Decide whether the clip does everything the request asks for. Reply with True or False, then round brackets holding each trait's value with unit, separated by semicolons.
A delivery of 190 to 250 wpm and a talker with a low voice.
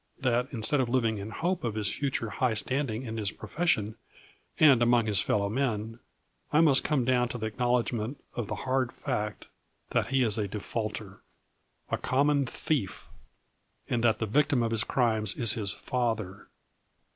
False (170 wpm; 115 Hz)